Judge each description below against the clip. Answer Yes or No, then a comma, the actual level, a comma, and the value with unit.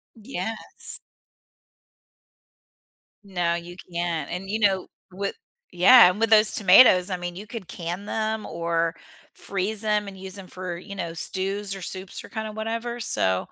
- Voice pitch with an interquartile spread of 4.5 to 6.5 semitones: No, average, 3.3 semitones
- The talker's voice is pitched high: Yes, high, 195 Hz